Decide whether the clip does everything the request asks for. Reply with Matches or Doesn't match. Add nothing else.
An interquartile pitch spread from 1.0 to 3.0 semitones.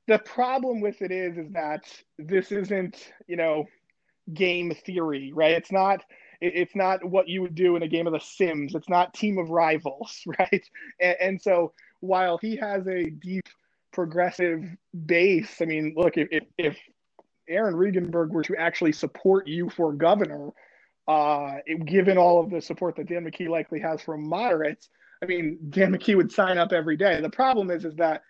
Matches